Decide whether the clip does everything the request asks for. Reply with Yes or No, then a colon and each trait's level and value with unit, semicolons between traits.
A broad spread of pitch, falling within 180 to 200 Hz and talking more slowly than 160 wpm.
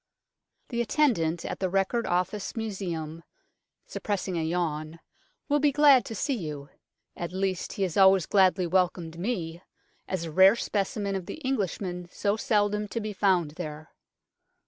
No: average, 3.7 semitones; high, 190 Hz; average, 150 wpm